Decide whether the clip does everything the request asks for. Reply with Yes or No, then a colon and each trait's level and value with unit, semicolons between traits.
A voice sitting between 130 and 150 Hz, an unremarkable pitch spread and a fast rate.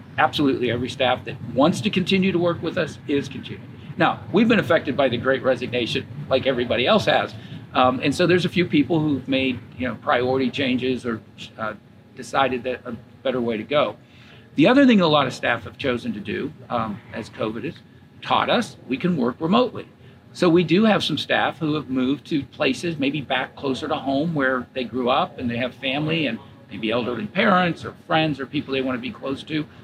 Yes: low, 135 Hz; average, 3.9 semitones; fast, 215 wpm